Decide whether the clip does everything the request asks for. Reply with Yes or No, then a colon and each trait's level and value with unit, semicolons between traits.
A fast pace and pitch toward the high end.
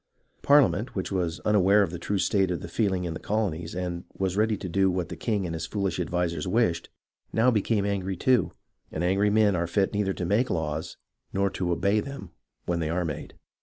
No: fast, 220 wpm; very low, 95 Hz